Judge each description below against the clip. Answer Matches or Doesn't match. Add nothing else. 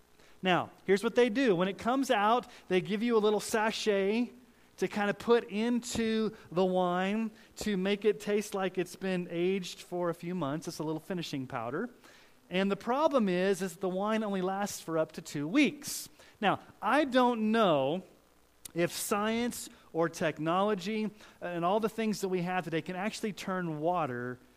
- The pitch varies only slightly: Doesn't match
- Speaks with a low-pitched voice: Doesn't match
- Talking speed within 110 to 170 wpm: Doesn't match